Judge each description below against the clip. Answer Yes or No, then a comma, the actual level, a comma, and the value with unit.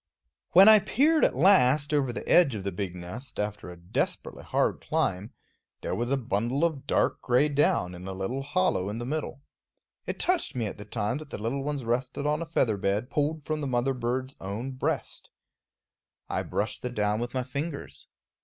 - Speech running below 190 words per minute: No, average, 200 wpm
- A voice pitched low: Yes, low, 125 Hz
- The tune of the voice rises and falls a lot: Yes, wide, 5.8 semitones